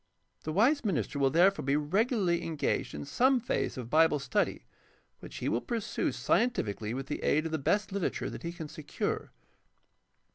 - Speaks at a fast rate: No, average, 180 wpm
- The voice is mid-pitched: Yes, medium, 165 Hz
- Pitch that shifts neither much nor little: No, wide, 6.2 semitones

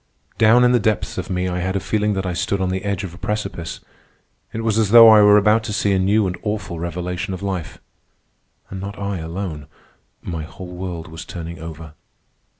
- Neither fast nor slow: No, fast, 215 wpm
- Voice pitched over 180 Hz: No, very low, 95 Hz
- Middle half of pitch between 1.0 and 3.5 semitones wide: Yes, average, 3.1 semitones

